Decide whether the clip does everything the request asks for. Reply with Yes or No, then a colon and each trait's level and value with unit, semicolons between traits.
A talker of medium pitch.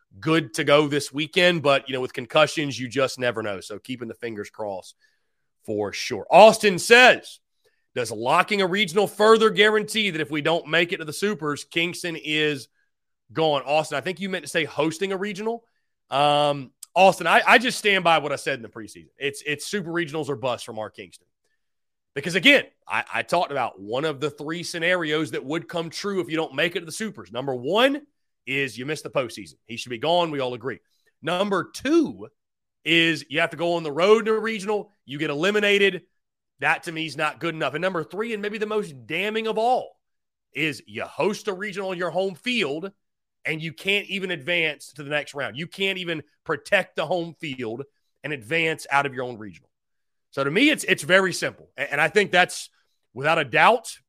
Yes: medium, 165 Hz